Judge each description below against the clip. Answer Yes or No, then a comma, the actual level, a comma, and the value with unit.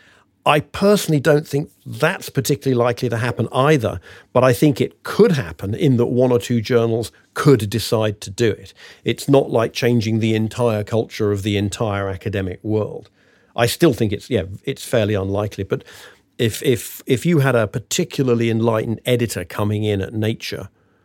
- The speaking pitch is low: Yes, low, 115 Hz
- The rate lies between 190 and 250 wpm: No, average, 175 wpm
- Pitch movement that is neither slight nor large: Yes, average, 3.7 semitones